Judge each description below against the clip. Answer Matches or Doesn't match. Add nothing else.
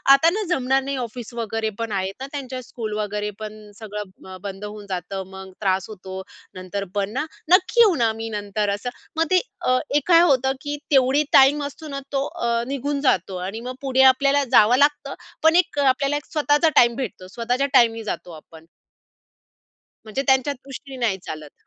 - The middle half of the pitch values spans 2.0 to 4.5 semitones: Doesn't match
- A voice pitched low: Doesn't match